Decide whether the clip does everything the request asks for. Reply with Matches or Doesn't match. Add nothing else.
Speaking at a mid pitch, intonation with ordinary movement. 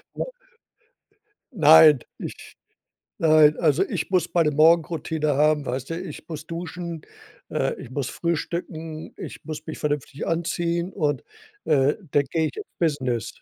Doesn't match